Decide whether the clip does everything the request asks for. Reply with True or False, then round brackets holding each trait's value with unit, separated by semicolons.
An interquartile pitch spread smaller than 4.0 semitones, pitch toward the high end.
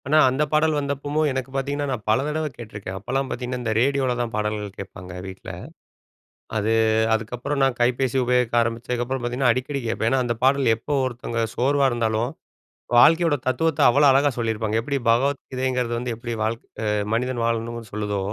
False (3.1 semitones; 125 Hz)